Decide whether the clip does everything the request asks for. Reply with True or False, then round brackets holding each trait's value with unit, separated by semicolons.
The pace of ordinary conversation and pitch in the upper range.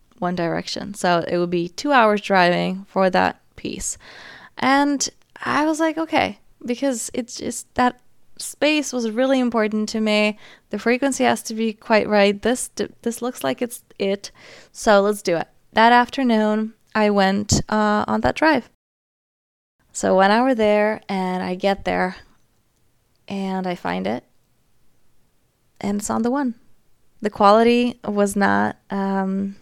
True (150 wpm; 210 Hz)